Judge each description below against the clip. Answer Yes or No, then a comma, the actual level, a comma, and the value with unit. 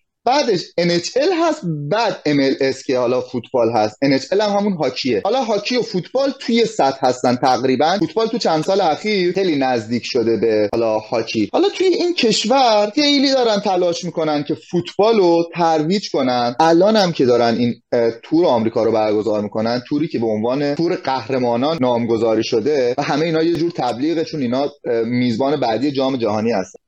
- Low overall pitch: No, medium, 155 Hz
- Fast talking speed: Yes, fast, 170 wpm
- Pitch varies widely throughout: Yes, wide, 8.0 semitones